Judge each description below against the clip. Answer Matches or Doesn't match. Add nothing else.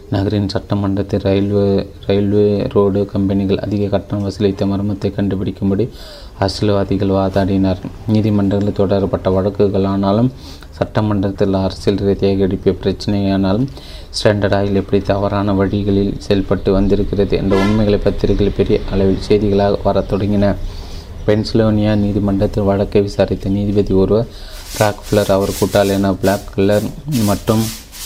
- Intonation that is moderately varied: Doesn't match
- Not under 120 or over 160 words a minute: Doesn't match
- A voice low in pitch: Matches